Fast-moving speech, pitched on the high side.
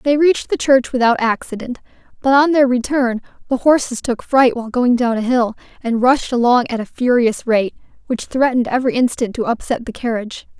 No: average, 195 wpm; high, 245 Hz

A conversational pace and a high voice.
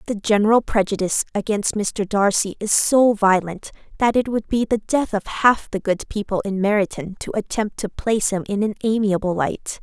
Yes: average, 190 wpm; high, 205 Hz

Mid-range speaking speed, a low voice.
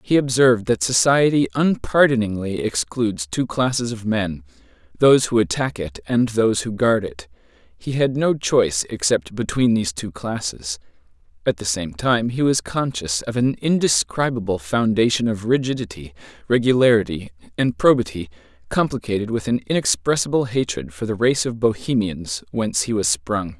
Yes: average, 145 wpm; low, 110 Hz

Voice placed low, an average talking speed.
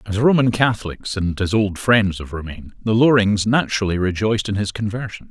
Yes: low, 105 Hz; average, 180 wpm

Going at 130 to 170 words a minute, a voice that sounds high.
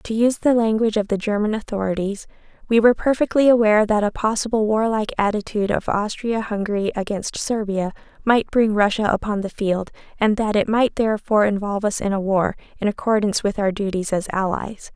No: average, 180 wpm; high, 210 Hz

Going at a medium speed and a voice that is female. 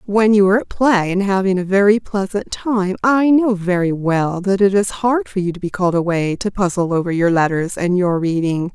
No: fast, 225 wpm; female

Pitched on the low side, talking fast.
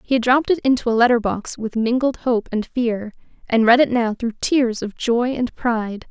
No: high, 235 Hz; fast, 225 wpm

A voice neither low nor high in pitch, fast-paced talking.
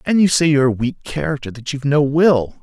Yes: medium, 145 Hz; fast, 250 wpm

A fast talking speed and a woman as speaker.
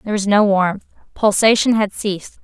No: average, 170 wpm; female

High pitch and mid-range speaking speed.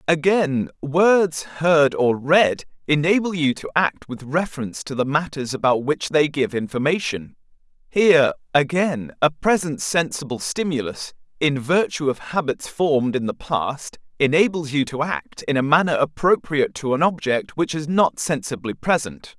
No: medium, 150 Hz; average, 150 wpm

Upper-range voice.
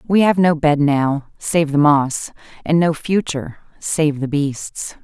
No: medium, 150 Hz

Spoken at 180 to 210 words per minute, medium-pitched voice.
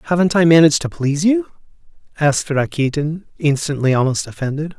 No: average, 140 wpm; medium, 155 Hz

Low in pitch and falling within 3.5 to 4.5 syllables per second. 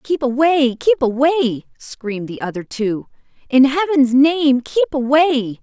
No: very high, 270 Hz; 4.2 syllables/s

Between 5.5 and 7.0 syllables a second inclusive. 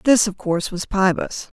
No: 5.0 syllables/s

